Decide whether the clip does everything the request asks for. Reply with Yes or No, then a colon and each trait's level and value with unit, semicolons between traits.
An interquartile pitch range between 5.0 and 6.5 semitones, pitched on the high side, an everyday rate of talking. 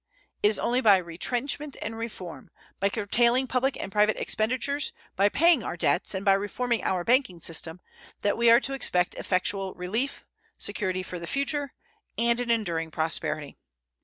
Yes: average, 5.3 semitones; high, 210 Hz; average, 160 wpm